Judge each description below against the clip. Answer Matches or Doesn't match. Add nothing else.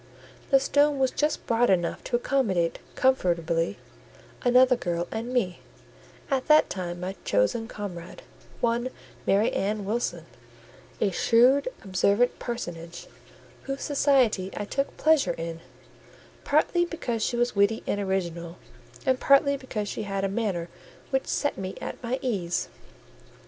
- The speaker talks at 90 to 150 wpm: Matches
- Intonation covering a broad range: Matches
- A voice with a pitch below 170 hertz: Doesn't match